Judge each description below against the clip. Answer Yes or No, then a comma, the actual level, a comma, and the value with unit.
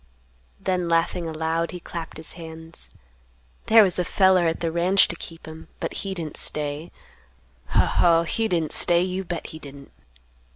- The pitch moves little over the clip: Yes, narrow, 1.9 semitones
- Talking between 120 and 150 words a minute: No, average, 170 wpm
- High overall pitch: No, medium, 170 Hz